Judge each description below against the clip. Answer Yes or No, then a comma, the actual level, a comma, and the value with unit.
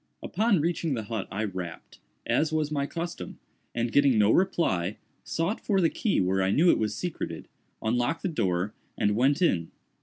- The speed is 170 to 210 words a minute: Yes, average, 180 wpm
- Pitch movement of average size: No, wide, 8.7 semitones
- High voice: No, low, 120 Hz